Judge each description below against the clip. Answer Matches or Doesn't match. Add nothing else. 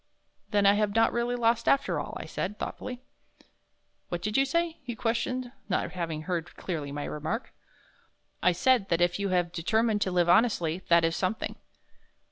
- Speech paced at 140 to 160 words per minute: Doesn't match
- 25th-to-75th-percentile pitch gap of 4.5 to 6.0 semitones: Matches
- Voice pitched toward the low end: Doesn't match